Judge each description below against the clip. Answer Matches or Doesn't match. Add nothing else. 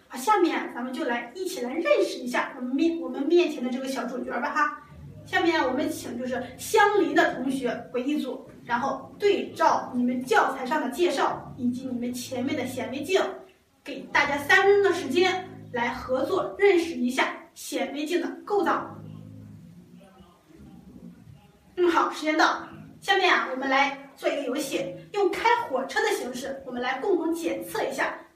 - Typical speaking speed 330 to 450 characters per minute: Doesn't match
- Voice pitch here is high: Matches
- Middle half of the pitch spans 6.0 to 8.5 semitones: Doesn't match